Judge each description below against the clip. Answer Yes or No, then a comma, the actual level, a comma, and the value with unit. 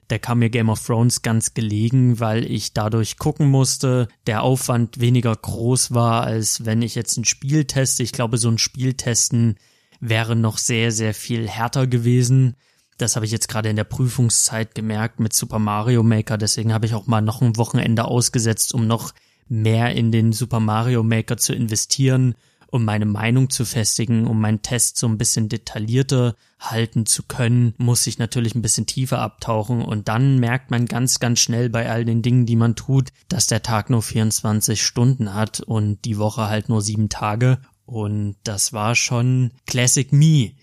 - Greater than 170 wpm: Yes, average, 185 wpm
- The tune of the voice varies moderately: No, narrow, 2.0 semitones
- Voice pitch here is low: Yes, low, 115 Hz